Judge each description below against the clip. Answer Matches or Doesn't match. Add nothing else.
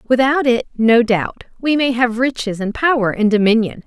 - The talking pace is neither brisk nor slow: Matches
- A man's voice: Doesn't match